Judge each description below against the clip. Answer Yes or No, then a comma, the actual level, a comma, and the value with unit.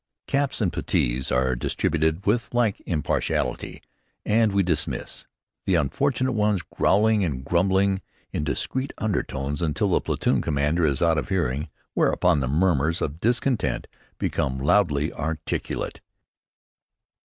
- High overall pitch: No, very low, 85 Hz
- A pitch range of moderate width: No, wide, 6.1 semitones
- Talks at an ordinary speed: No, slow, 125 wpm